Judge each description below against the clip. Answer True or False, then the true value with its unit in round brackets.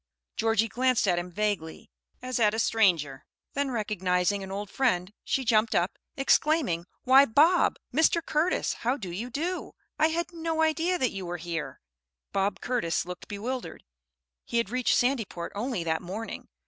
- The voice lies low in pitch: False (225 Hz)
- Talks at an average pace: True (160 wpm)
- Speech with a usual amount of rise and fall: False (6.7 semitones)